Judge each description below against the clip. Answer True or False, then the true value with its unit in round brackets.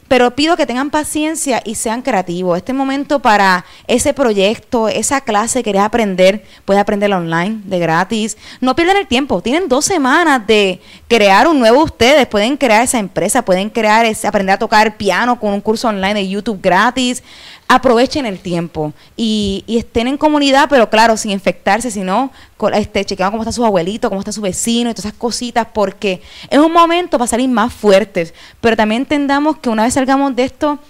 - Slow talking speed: False (190 wpm)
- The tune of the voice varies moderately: True (4.5 semitones)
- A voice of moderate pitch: False (225 Hz)